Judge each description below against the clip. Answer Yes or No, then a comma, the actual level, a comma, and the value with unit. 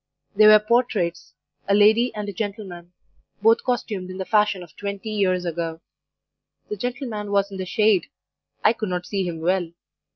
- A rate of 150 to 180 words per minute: Yes, average, 170 wpm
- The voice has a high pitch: Yes, high, 200 Hz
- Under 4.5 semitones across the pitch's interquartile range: Yes, average, 2.9 semitones